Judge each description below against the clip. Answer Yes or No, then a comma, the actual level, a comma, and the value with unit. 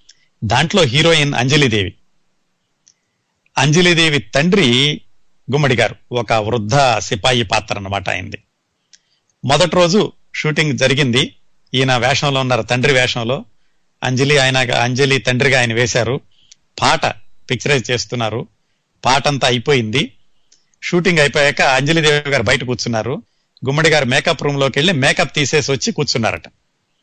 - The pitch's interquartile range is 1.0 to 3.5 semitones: Yes, average, 3.2 semitones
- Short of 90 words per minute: No, average, 110 wpm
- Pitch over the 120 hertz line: Yes, low, 135 Hz